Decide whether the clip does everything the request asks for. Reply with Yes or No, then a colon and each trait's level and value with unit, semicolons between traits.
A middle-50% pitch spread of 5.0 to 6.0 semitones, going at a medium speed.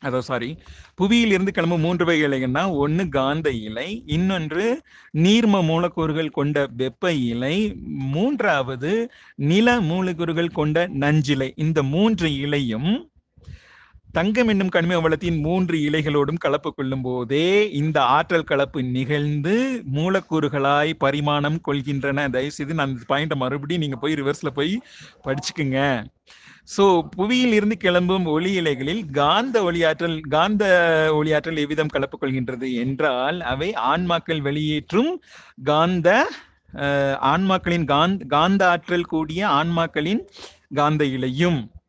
No: average, 4.2 semitones; average, 110 wpm